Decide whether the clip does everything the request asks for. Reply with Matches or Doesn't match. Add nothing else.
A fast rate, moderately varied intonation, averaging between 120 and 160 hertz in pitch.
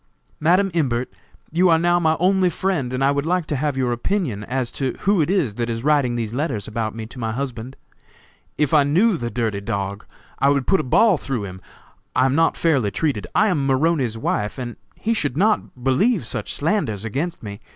Doesn't match